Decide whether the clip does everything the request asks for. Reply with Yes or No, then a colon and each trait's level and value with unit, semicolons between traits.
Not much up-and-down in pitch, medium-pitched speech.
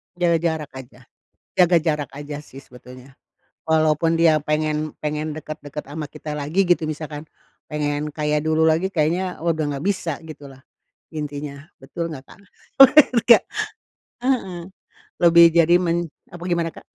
Yes: narrow, 2.3 semitones; medium, 155 Hz